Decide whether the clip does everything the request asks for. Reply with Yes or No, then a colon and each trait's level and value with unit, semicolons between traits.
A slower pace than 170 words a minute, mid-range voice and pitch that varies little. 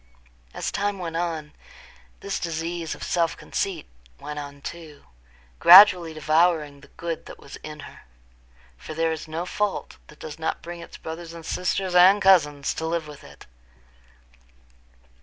Yes: average, 155 wpm; medium, 165 Hz; narrow, 2.3 semitones